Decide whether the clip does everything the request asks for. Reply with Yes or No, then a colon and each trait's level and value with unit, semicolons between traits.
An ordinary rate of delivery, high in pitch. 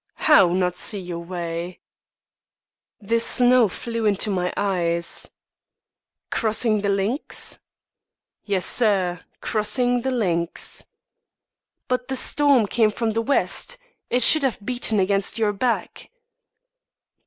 No: slow, 115 wpm; high, 210 Hz